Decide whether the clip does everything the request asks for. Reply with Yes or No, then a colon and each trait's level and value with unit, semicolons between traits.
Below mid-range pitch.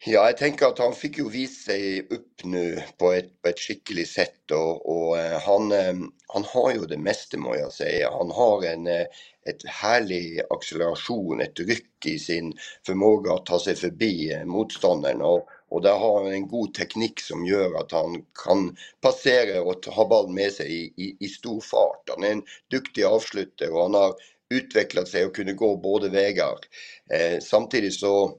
Yes: low, 100 Hz